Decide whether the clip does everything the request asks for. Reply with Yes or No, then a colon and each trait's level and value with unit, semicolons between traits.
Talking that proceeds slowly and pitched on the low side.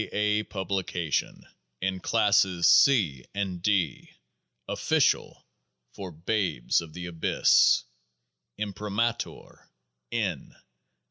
Yes: slow, 80 wpm; very low, 95 Hz